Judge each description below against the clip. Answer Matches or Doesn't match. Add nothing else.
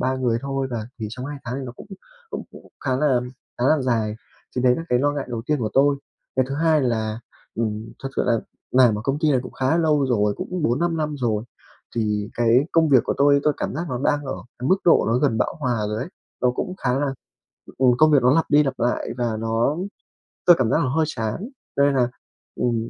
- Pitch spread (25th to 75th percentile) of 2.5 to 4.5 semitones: Matches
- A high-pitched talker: Doesn't match